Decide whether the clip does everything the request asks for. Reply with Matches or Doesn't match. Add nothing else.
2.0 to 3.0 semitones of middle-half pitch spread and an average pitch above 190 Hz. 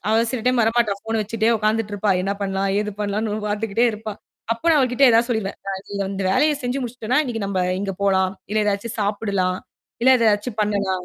Matches